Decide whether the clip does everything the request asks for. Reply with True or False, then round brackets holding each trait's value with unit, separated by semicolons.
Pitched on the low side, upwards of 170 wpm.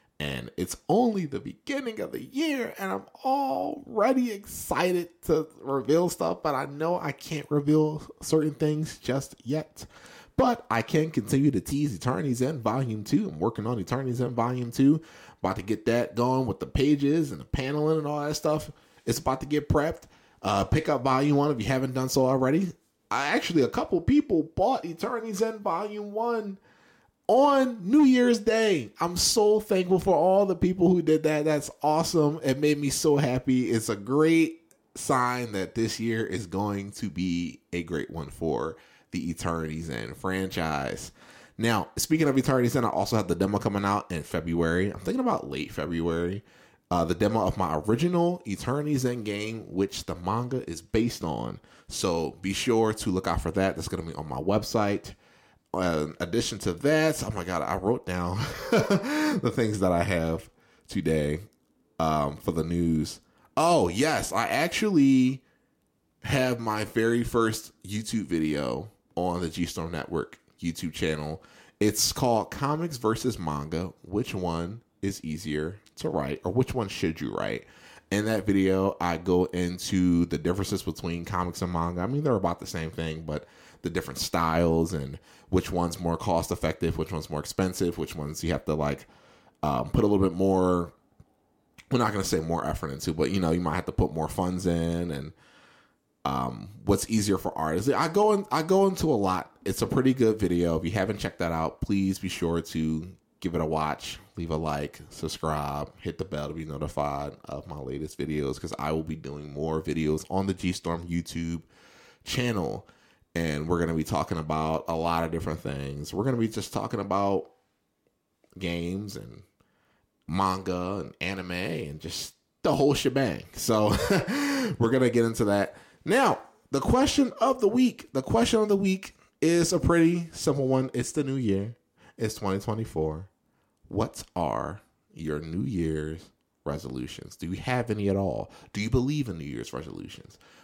True (100 Hz; 180 wpm)